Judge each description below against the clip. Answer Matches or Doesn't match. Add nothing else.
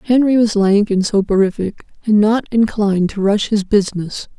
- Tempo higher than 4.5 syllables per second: Matches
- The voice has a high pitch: Matches